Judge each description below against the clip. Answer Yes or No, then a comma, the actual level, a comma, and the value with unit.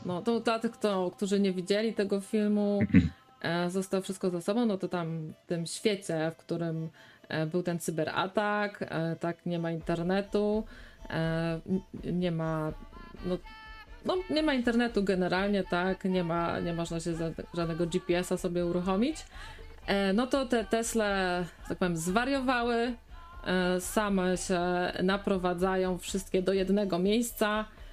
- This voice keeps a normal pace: Yes, average, 145 wpm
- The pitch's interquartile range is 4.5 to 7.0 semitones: No, average, 3.3 semitones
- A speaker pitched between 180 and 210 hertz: Yes, medium, 185 Hz